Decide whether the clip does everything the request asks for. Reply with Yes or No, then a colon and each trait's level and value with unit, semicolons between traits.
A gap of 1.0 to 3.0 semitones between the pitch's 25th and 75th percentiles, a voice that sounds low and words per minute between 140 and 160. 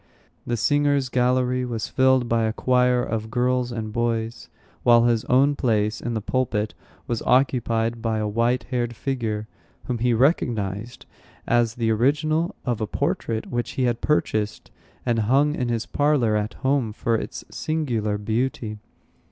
Yes: narrow, 2.4 semitones; low, 120 Hz; average, 155 wpm